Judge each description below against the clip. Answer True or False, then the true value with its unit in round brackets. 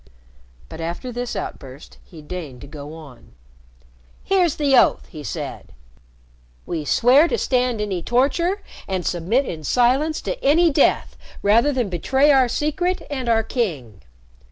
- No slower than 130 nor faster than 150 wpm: True (145 wpm)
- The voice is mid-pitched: False (240 Hz)